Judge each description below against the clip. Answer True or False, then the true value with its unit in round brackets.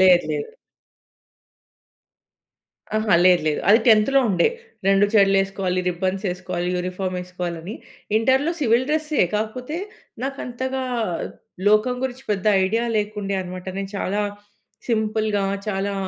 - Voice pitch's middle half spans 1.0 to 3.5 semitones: False (4.0 semitones)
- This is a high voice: True (205 Hz)